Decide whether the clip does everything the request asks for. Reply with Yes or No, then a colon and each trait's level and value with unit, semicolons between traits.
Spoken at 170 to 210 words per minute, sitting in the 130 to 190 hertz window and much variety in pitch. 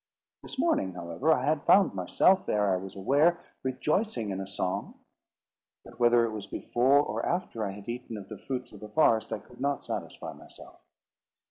No: average, 190 wpm; low, 120 Hz; wide, 6.3 semitones